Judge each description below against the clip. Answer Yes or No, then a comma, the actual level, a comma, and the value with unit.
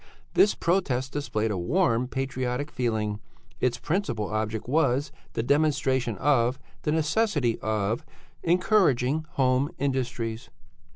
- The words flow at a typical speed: No, slow, 110 wpm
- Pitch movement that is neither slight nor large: Yes, average, 4.5 semitones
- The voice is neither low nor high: No, low, 130 Hz